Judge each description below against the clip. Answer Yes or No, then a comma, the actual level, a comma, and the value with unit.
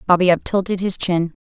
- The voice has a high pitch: No, medium, 180 Hz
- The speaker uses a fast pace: No, average, 170 wpm